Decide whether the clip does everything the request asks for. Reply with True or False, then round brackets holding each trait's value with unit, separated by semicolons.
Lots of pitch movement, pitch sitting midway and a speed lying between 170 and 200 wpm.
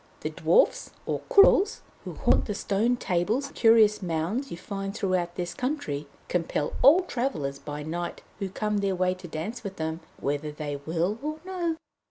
False (6.8 semitones; 195 Hz; 175 wpm)